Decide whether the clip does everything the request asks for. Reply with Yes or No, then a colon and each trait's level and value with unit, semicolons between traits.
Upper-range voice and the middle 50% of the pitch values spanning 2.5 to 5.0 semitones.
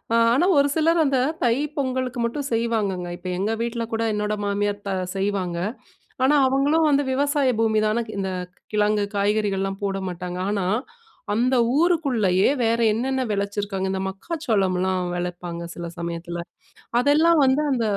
No: high, 215 Hz; wide, 5.4 semitones